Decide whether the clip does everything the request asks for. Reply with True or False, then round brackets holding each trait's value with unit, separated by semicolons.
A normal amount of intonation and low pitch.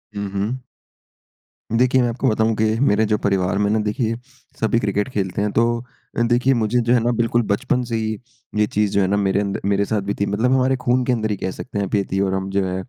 True (3.0 semitones; 105 Hz)